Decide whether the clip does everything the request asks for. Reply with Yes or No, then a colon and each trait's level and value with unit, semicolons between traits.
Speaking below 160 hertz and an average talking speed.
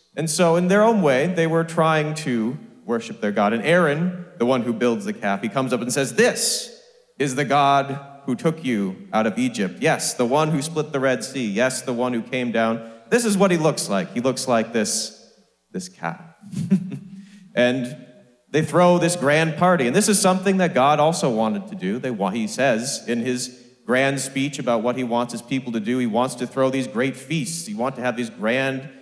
No: medium, 140 Hz; fast, 220 wpm